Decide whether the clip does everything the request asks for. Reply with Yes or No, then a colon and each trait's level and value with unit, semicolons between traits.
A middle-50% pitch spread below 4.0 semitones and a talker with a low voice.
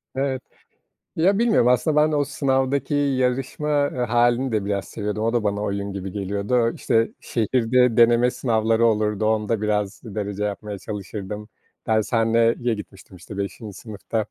Yes: average, 3.4 semitones; low, 115 Hz